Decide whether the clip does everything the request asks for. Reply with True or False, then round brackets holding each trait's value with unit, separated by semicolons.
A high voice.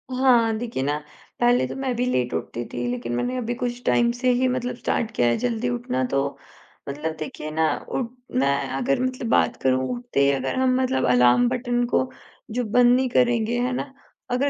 True (240 Hz)